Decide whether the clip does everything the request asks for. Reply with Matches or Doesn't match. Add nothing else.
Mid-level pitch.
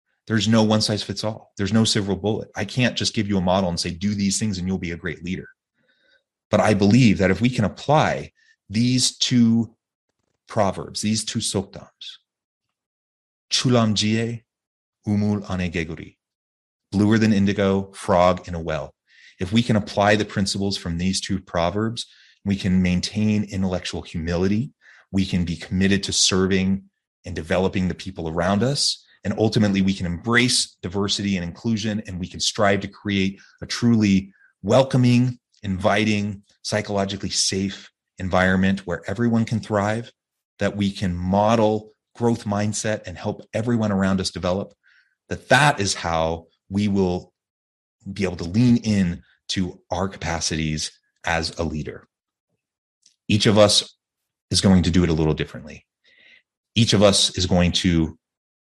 Doesn't match